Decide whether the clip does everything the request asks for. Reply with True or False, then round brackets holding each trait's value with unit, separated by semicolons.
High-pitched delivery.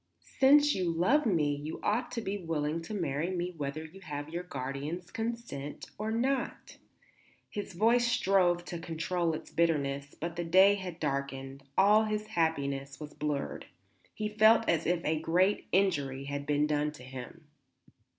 False (170 Hz)